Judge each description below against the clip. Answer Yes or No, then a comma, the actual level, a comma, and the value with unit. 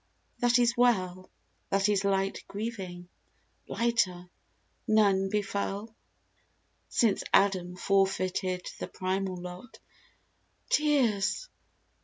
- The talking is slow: Yes, slow, 90 wpm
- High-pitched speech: Yes, high, 195 Hz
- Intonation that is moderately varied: Yes, average, 3.3 semitones